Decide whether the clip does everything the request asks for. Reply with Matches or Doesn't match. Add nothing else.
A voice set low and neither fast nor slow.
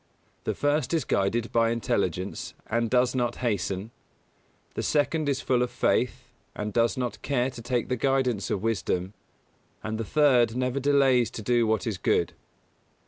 Matches